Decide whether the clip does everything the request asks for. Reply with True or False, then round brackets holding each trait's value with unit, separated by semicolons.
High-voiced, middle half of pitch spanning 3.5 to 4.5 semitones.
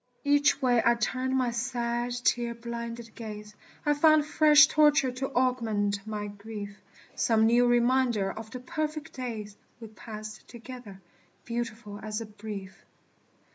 False (235 Hz; 3.0 semitones)